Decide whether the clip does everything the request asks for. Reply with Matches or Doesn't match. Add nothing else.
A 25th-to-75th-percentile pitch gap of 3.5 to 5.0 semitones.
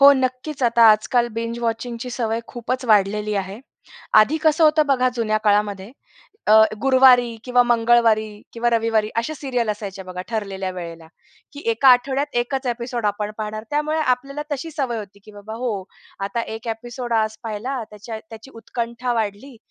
Doesn't match